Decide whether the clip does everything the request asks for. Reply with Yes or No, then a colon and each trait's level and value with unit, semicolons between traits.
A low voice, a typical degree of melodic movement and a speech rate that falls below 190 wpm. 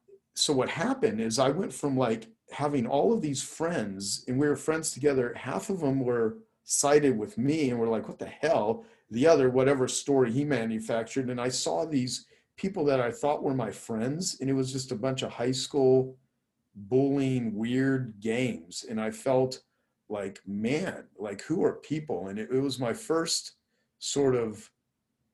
Yes: low, 130 Hz; average, 3.0 semitones; average, 180 wpm